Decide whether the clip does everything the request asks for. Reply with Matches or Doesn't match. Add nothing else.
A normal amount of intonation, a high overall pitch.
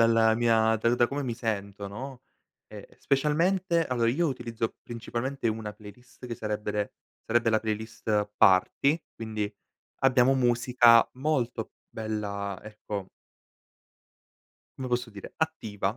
Doesn't match